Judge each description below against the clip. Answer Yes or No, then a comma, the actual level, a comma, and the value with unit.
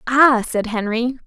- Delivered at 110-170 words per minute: Yes, average, 140 wpm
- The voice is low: No, high, 240 Hz